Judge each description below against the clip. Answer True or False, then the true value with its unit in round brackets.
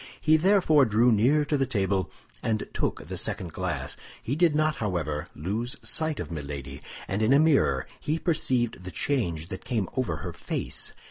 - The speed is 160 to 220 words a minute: True (180 wpm)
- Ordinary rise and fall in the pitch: False (8.3 semitones)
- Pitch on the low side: True (115 Hz)